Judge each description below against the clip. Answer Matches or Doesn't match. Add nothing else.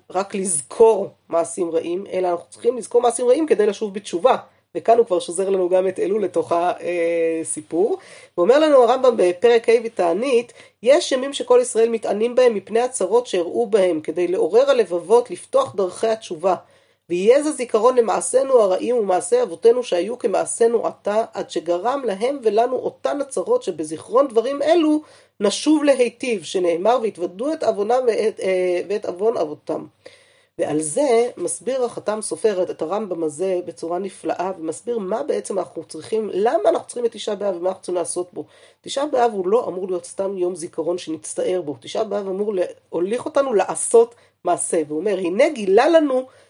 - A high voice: Matches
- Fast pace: Matches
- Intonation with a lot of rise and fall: Matches